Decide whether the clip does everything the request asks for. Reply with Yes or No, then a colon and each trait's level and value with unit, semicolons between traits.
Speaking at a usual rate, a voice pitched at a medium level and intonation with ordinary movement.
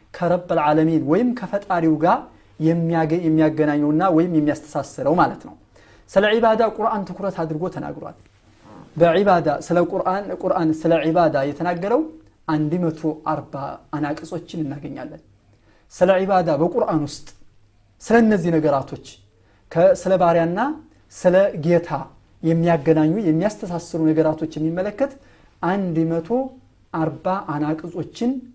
Yes: average, 90 wpm; medium, 165 Hz; average, 3.3 semitones